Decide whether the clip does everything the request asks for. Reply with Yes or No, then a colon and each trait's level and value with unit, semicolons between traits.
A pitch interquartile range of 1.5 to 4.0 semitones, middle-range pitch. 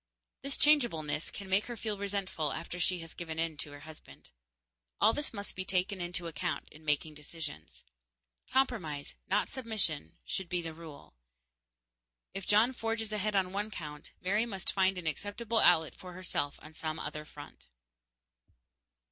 No: average, 4.8 semitones; medium, 180 Hz